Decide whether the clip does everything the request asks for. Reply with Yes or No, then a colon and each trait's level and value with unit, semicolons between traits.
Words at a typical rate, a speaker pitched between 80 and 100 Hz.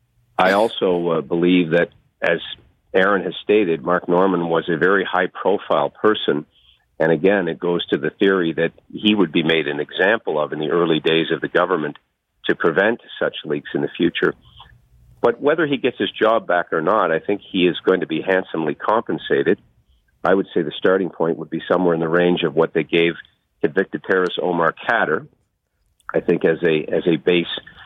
Yes: average, 195 wpm; very low, 85 Hz